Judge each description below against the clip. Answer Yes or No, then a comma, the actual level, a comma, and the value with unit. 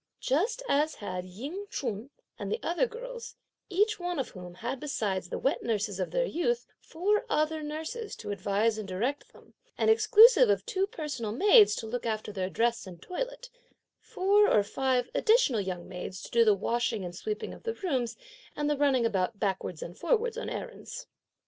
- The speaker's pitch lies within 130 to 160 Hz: No, very high, 265 Hz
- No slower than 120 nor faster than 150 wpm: No, average, 185 wpm